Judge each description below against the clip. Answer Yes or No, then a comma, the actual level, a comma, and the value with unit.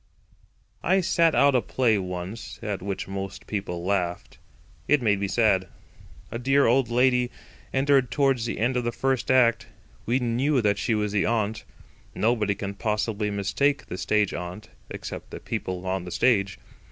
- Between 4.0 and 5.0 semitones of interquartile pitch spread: Yes, average, 4.5 semitones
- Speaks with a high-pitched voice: No, low, 110 Hz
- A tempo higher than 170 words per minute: No, average, 160 wpm